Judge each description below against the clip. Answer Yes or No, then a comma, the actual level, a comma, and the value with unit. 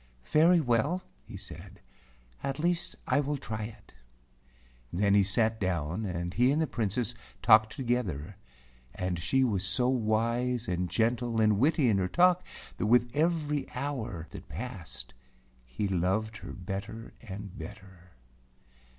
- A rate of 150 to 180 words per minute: No, average, 140 wpm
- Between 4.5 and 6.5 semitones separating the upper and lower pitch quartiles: Yes, average, 5.1 semitones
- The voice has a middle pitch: No, low, 110 Hz